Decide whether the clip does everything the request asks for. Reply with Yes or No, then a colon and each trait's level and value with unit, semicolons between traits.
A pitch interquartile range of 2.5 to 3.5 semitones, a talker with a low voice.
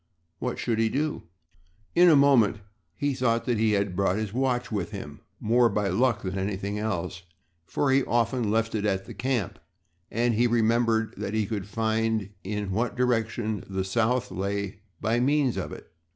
Yes: average, 3.2 semitones; low, 110 Hz